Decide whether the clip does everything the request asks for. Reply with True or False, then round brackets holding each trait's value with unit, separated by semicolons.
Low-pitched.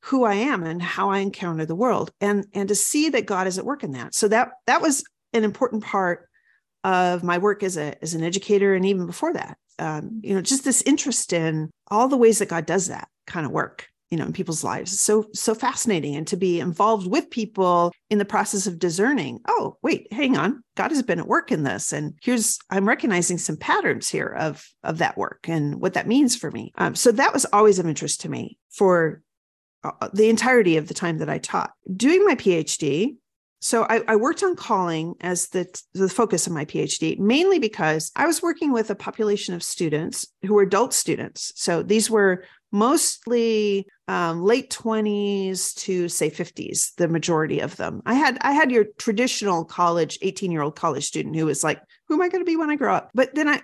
False (205 Hz)